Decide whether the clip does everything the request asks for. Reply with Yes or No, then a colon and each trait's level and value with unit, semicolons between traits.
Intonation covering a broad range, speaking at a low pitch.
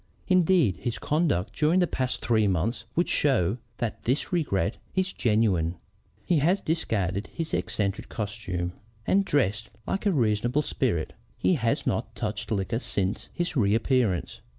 Yes: wide, 7.7 semitones; low, 115 Hz